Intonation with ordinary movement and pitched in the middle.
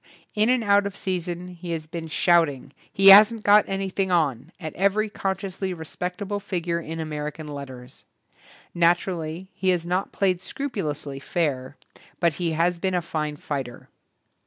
Yes: average, 3.7 semitones; medium, 175 Hz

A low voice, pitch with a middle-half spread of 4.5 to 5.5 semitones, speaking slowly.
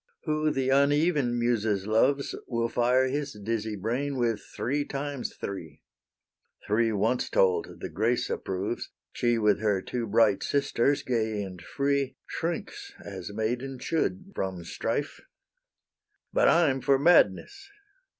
Yes: low, 120 Hz; average, 4.8 semitones; slow, 130 wpm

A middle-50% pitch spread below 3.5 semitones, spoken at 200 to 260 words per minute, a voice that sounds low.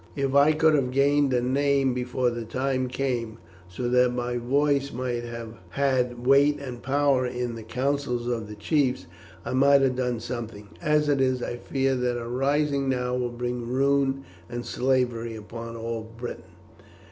No: narrow, 2.4 semitones; average, 170 wpm; low, 125 Hz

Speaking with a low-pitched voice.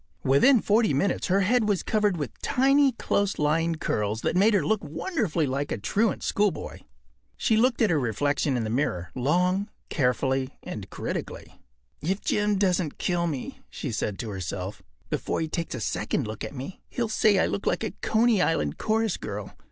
No: medium, 170 Hz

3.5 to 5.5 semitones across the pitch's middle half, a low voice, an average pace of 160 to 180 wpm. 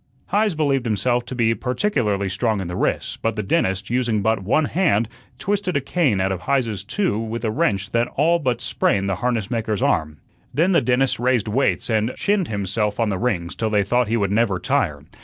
No: average, 4.4 semitones; low, 115 Hz; fast, 205 wpm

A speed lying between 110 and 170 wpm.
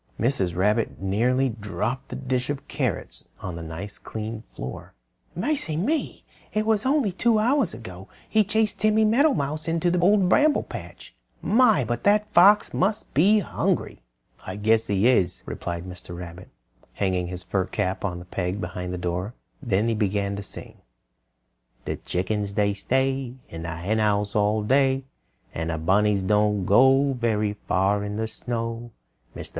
Yes: average, 165 wpm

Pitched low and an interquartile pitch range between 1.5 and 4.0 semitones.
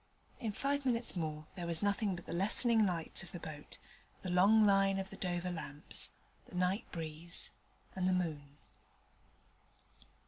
No: medium, 180 Hz; average, 3.3 semitones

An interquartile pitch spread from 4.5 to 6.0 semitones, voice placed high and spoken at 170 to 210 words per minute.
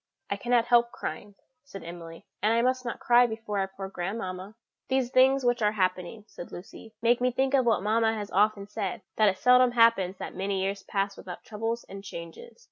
No: average, 3.7 semitones; high, 215 Hz; fast, 205 wpm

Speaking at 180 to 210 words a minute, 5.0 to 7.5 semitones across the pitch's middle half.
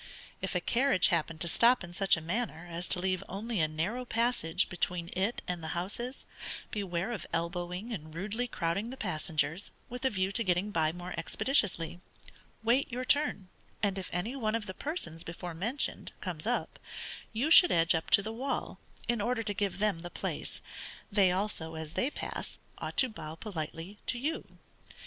Yes: average, 185 wpm; wide, 5.4 semitones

